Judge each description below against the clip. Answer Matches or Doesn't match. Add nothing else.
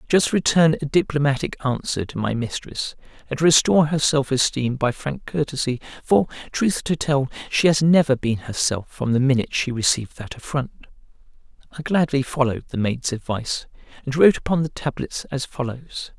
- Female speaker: Doesn't match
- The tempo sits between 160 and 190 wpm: Matches